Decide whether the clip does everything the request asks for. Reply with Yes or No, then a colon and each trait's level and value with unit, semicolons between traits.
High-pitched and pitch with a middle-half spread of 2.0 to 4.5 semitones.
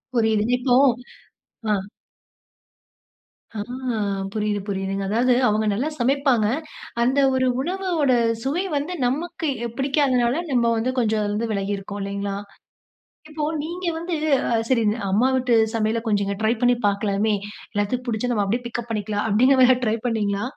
Yes: high, 235 Hz; average, 4.0 semitones